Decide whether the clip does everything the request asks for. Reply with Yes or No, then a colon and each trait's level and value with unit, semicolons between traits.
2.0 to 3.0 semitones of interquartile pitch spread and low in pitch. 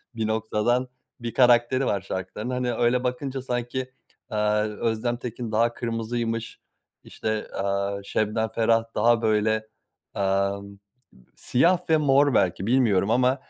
Yes: average, 2.7 semitones; low, 115 Hz